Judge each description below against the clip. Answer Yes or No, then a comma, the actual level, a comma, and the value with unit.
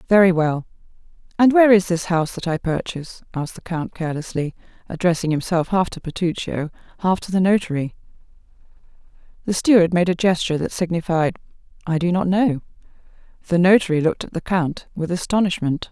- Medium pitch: Yes, medium, 175 Hz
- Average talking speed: Yes, average, 160 wpm